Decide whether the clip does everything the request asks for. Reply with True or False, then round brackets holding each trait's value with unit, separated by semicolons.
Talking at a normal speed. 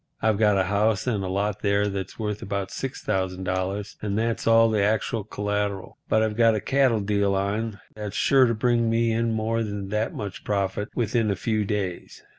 True (190 wpm)